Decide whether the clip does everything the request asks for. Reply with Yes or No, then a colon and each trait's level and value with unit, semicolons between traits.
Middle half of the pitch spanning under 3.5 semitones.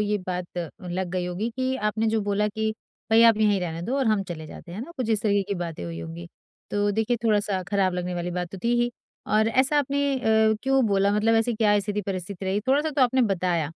No: average, 3.9 semitones